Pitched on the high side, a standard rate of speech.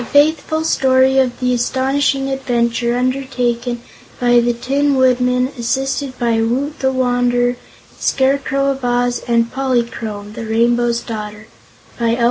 Yes: high, 245 Hz; average, 145 wpm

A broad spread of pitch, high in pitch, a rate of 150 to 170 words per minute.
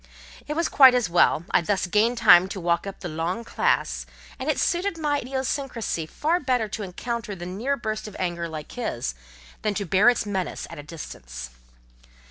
No: wide, 6.3 semitones; high, 205 Hz; average, 190 wpm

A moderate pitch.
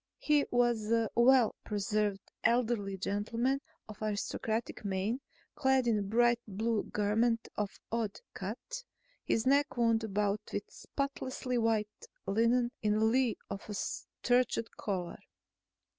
No: high, 225 Hz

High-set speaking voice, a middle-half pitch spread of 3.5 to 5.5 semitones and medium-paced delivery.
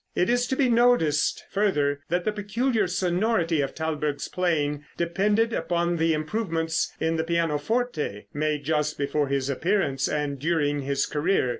No: medium, 165 Hz; average, 5.2 semitones; average, 150 wpm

